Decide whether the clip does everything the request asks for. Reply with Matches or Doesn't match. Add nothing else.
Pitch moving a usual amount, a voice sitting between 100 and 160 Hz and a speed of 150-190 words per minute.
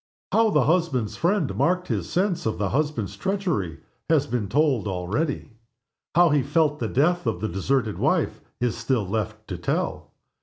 Doesn't match